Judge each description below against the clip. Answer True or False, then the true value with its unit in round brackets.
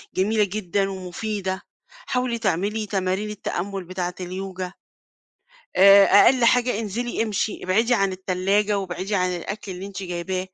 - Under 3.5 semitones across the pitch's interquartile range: True (2.4 semitones)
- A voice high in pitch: True (195 Hz)